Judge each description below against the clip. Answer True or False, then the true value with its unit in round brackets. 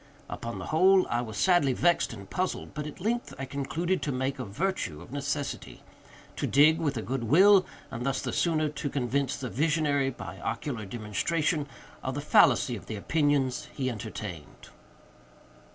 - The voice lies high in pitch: False (140 Hz)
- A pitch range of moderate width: True (4.5 semitones)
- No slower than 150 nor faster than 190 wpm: True (170 wpm)